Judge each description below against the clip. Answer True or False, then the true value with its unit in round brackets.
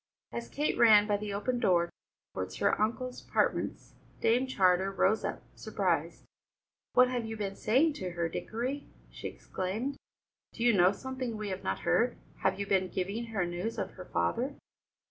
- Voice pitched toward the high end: True (215 Hz)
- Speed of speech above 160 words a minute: True (170 wpm)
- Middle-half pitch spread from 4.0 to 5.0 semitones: True (4.5 semitones)